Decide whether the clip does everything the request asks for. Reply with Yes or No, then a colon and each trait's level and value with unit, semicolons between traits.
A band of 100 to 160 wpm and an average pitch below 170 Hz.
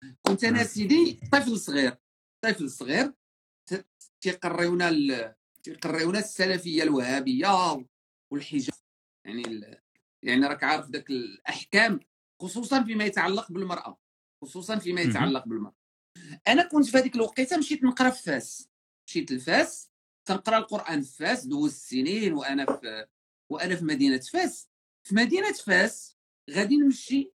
No: average, 120 wpm; high, 190 Hz